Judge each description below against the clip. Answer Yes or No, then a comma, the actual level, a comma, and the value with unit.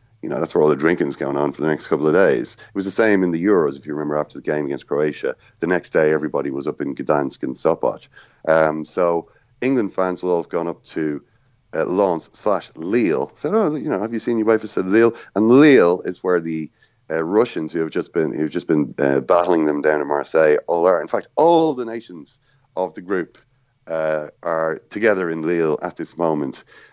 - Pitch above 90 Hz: No, very low, 80 Hz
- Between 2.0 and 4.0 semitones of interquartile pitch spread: No, average, 5.3 semitones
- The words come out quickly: Yes, fast, 230 wpm